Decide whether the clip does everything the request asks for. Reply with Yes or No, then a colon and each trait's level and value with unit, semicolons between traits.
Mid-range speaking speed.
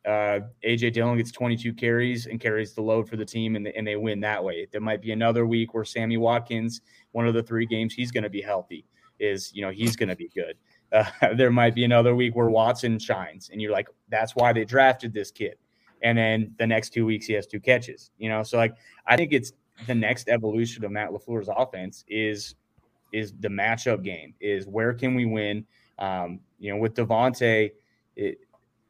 No: fast, 215 wpm